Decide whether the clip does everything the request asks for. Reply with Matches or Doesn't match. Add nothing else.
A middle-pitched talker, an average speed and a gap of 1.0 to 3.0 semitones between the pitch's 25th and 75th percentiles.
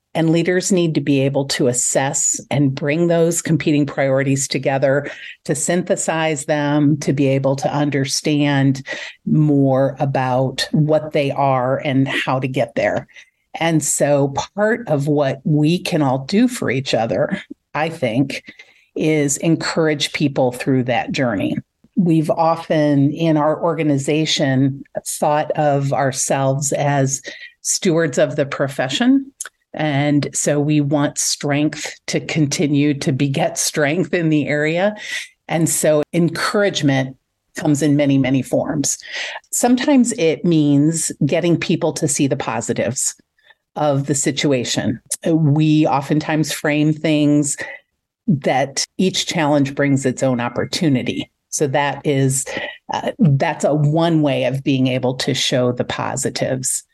Doesn't match